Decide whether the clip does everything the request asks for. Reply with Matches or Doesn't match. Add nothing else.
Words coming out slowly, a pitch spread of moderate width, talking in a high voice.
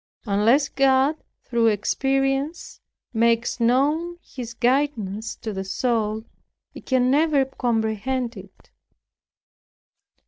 Matches